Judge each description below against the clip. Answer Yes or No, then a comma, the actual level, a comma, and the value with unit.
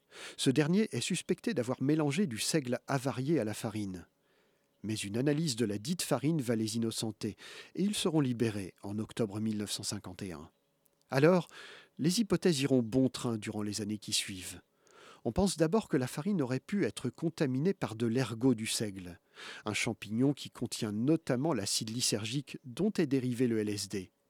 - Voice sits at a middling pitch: No, low, 125 Hz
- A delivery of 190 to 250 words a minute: No, average, 165 wpm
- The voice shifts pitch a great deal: Yes, wide, 6.2 semitones